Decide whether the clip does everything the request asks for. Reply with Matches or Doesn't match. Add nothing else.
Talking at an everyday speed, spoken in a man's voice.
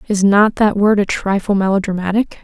Doesn't match